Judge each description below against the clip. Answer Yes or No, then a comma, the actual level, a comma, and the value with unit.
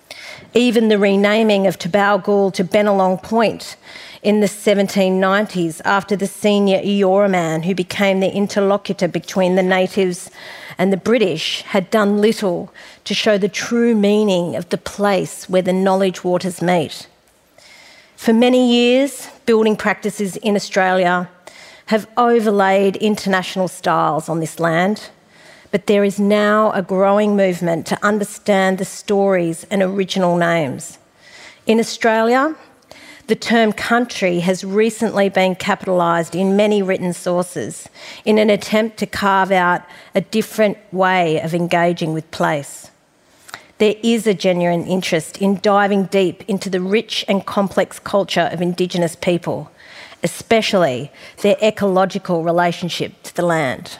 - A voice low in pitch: No, high, 195 Hz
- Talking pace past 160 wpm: No, slow, 135 wpm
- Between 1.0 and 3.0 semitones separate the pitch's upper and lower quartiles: Yes, narrow, 2.6 semitones